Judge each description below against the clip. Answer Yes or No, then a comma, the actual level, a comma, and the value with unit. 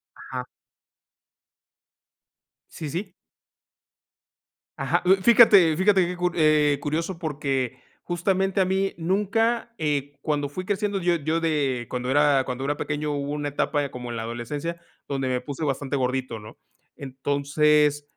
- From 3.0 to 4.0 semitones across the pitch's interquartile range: No, average, 4.5 semitones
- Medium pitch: Yes, medium, 150 Hz